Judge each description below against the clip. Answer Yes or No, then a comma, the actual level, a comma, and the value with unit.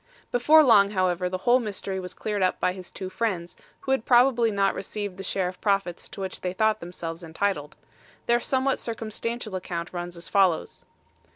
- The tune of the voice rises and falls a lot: No, average, 4.0 semitones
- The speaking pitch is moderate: No, high, 195 Hz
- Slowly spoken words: No, average, 190 wpm